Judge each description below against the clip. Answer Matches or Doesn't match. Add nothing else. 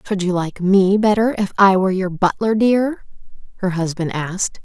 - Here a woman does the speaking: Matches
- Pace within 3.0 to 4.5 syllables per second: Doesn't match